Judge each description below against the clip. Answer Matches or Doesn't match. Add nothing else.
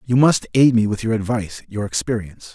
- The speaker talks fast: Matches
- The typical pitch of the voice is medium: Doesn't match